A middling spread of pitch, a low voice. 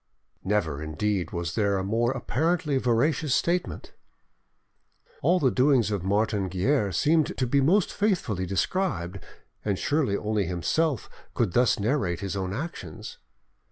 No: wide, 7.3 semitones; low, 110 Hz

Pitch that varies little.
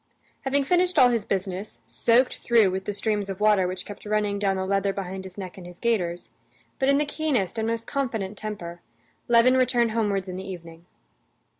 No: average, 3.7 semitones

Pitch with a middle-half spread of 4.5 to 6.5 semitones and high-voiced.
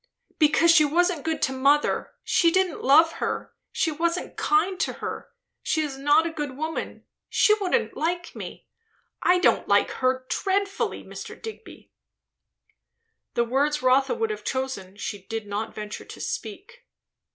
Yes: average, 5.3 semitones; very high, 310 Hz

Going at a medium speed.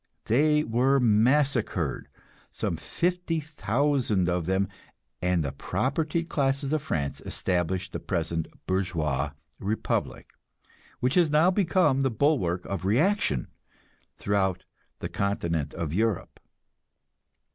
No: slow, 105 wpm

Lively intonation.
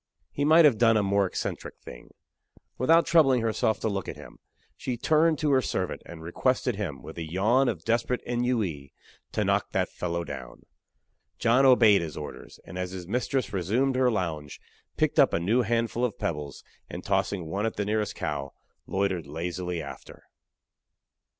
Yes: wide, 6.4 semitones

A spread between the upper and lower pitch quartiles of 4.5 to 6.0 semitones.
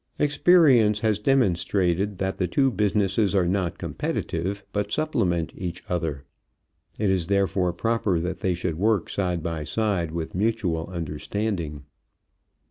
No: average, 3.7 semitones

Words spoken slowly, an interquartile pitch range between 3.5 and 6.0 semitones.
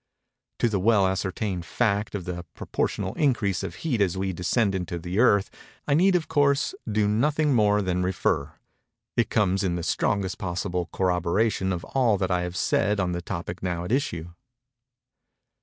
No: average, 170 wpm; average, 4.0 semitones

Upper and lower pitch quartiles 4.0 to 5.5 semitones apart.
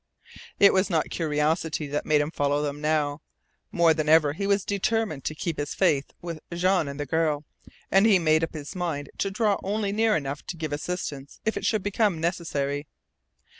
Yes: average, 4.4 semitones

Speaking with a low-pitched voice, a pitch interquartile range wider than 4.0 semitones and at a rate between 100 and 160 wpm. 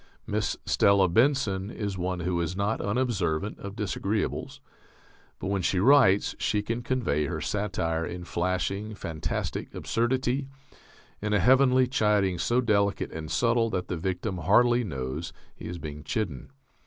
Yes: low, 100 Hz; average, 4.7 semitones; average, 145 wpm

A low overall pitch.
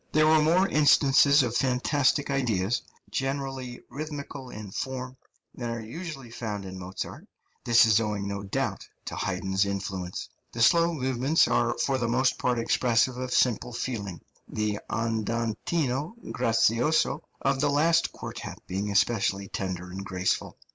Yes: low, 120 Hz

